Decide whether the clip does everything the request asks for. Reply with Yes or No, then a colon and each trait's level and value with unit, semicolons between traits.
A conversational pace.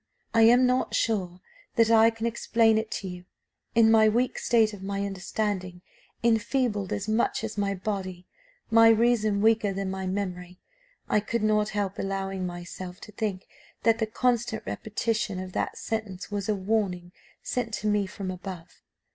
Yes: average, 165 wpm